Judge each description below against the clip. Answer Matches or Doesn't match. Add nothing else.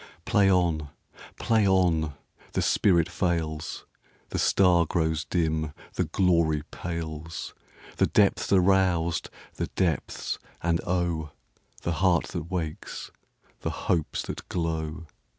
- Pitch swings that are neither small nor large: Doesn't match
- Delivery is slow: Matches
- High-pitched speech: Doesn't match